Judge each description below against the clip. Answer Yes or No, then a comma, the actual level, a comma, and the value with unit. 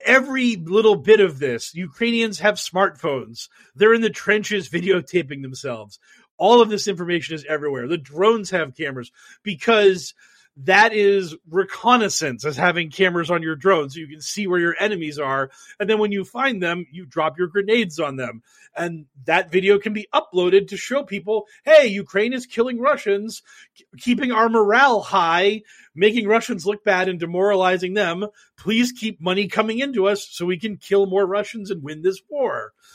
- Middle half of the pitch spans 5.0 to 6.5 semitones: No, average, 4.2 semitones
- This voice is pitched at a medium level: No, high, 195 Hz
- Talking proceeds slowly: No, average, 175 wpm